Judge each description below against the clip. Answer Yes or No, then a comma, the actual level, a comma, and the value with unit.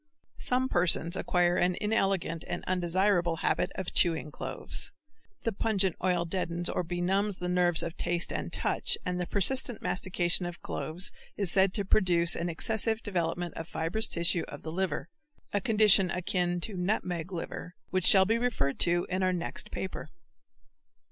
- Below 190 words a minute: Yes, average, 160 wpm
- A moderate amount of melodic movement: No, narrow, 2.1 semitones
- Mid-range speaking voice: Yes, medium, 180 Hz